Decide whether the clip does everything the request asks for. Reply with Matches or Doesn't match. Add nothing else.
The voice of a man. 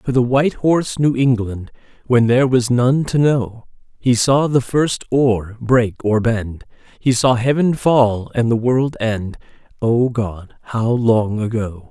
Matches